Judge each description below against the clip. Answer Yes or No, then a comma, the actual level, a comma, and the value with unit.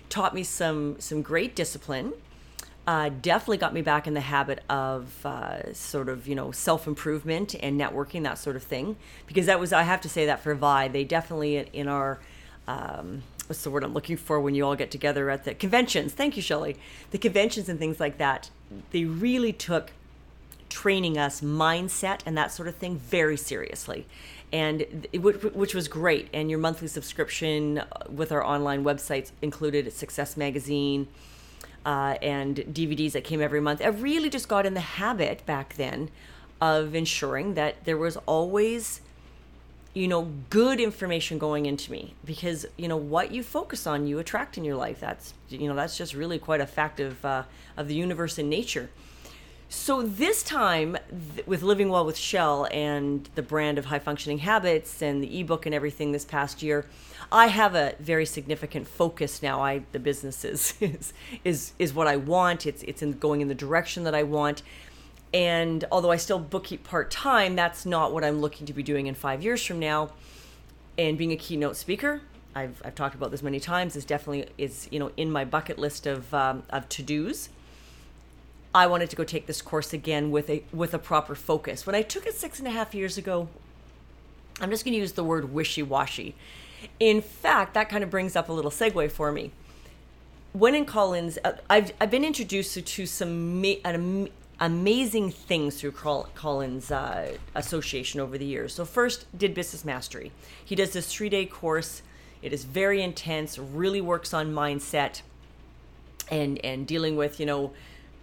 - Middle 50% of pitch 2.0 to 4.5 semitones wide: Yes, average, 3.9 semitones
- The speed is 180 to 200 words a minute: Yes, average, 190 wpm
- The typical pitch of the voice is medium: Yes, medium, 155 Hz